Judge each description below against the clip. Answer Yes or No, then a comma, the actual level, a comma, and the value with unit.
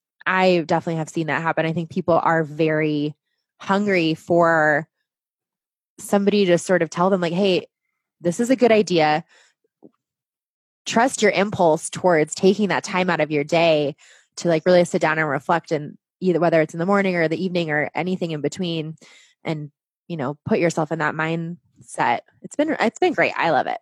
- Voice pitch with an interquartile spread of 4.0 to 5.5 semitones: No, average, 3.0 semitones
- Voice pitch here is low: No, medium, 170 Hz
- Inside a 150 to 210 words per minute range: Yes, average, 190 wpm